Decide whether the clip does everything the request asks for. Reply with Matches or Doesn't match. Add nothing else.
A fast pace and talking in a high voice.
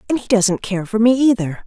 Matches